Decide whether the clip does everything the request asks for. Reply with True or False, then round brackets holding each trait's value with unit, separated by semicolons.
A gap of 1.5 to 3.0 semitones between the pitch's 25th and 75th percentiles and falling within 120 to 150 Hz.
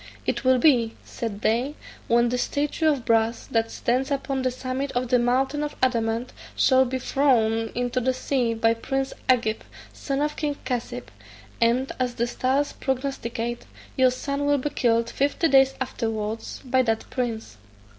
False (2.6 semitones; 255 Hz)